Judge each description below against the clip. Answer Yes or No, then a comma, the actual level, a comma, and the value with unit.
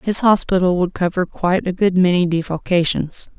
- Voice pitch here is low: No, medium, 180 Hz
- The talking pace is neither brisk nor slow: Yes, average, 160 wpm